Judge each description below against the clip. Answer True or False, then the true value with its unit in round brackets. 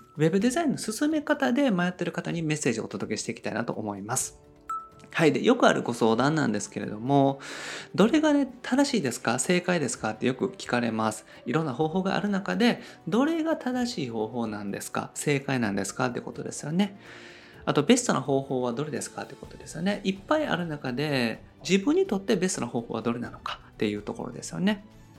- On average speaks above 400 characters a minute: True (430 characters per minute)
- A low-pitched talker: False (165 Hz)